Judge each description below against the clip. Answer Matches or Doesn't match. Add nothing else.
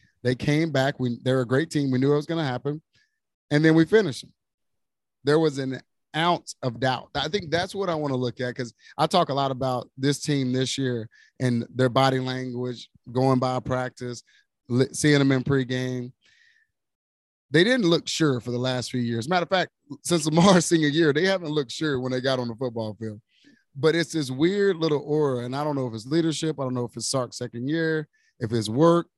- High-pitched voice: Doesn't match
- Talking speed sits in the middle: Doesn't match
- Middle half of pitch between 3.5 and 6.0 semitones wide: Matches